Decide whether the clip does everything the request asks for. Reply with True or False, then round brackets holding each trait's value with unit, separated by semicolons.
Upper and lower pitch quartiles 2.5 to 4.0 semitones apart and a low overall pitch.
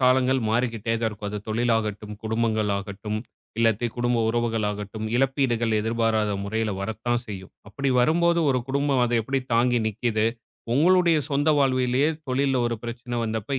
True (2.9 semitones; 115 Hz)